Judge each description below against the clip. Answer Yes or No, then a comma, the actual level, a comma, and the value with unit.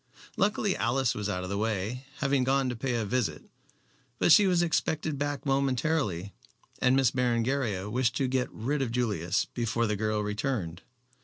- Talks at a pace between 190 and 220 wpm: No, average, 170 wpm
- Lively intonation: No, average, 4.2 semitones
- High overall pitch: No, low, 125 Hz